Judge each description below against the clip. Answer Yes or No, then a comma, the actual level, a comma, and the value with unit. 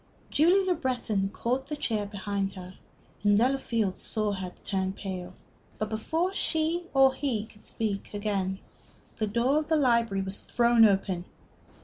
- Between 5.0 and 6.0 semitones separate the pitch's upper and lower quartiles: Yes, average, 5.3 semitones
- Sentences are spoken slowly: No, average, 150 wpm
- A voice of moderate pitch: No, high, 215 Hz